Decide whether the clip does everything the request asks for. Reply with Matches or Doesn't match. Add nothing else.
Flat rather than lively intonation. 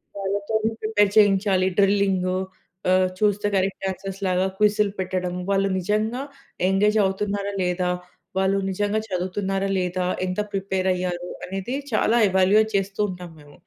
Matches